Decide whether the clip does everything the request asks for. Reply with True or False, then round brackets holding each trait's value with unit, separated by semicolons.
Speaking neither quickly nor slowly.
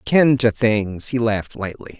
True (180 wpm)